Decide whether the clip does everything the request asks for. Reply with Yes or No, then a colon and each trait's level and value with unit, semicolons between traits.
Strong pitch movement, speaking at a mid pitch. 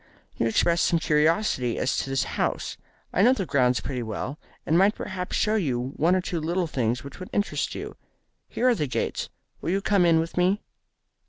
Yes: wide, 5.9 semitones; medium, 165 Hz